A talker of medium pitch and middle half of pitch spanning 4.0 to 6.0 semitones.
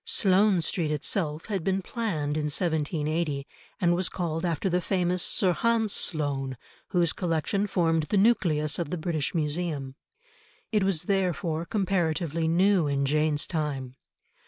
No: medium, 165 Hz; average, 3.6 semitones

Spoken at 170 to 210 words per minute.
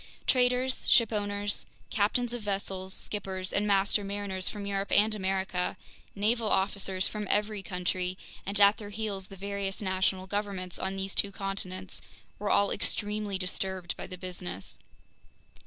No: average, 140 wpm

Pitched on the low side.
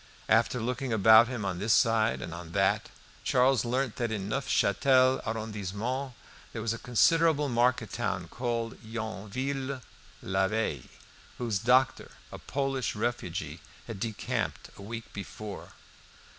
Yes: low, 115 Hz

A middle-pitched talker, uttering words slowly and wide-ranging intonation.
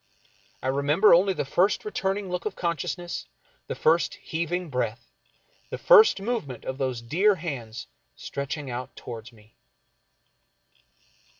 Yes: medium, 155 Hz; slow, 125 wpm; wide, 6.6 semitones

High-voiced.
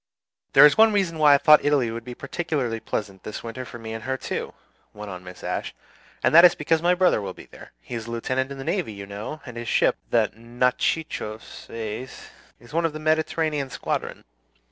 No: low, 130 Hz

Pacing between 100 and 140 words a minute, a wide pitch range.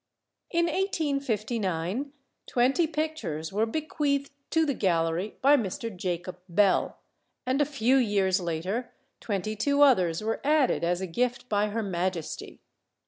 Yes: slow, 135 wpm; wide, 7.2 semitones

